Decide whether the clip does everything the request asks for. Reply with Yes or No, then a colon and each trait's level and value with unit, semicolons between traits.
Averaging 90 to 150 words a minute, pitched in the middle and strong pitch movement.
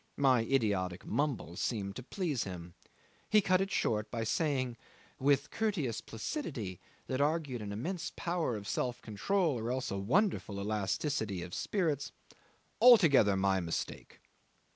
No: average, 140 wpm; low, 125 Hz; wide, 7.7 semitones